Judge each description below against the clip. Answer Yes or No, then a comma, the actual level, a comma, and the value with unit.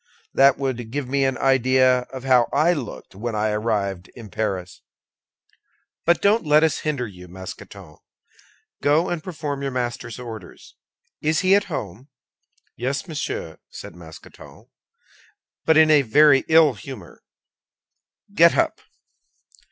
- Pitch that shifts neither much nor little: No, wide, 5.8 semitones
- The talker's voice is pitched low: Yes, low, 130 Hz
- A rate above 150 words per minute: No, slow, 135 wpm